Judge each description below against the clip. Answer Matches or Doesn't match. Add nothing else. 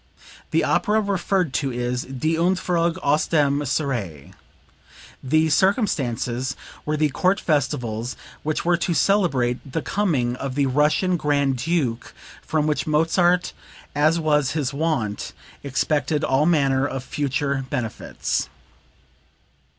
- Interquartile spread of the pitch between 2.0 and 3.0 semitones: Doesn't match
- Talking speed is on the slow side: Matches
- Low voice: Doesn't match